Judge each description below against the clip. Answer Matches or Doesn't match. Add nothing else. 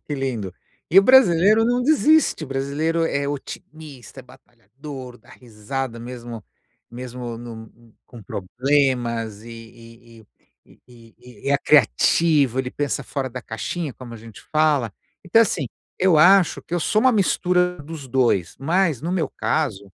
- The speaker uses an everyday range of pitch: Doesn't match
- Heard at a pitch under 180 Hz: Matches